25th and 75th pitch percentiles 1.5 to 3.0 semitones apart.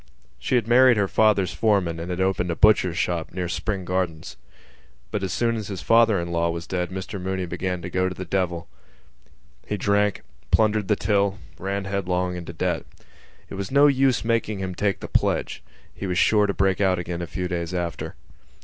Yes: average, 2.7 semitones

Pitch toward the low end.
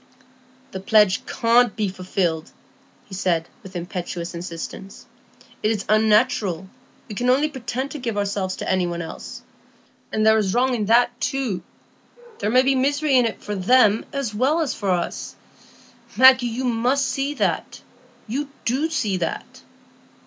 No: high, 220 Hz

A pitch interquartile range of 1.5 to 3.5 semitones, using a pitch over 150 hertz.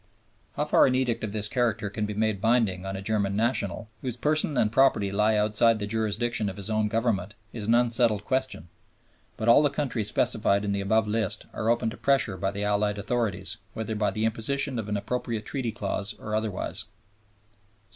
No: narrow, 2.5 semitones; low, 110 Hz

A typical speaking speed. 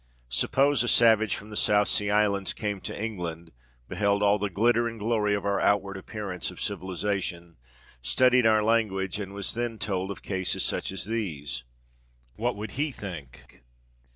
Yes: average, 155 wpm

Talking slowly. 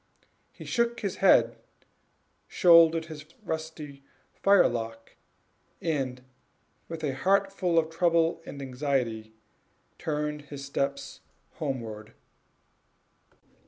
Yes: slow, 90 wpm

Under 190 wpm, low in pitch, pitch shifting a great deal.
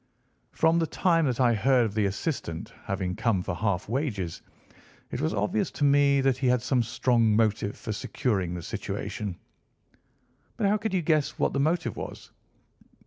Yes: average, 175 wpm; low, 120 Hz; wide, 5.8 semitones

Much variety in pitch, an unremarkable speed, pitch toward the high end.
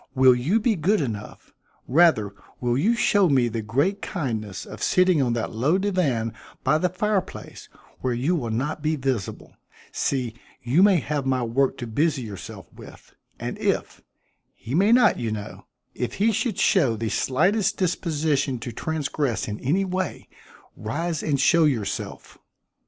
No: wide, 7.0 semitones; average, 160 wpm; medium, 140 Hz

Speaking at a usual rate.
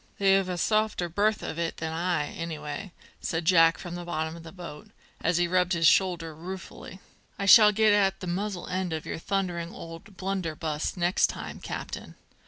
Yes: average, 185 wpm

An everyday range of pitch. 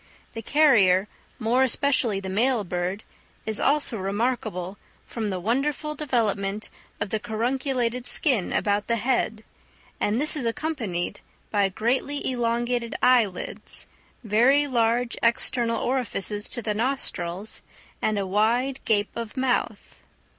Yes: average, 3.8 semitones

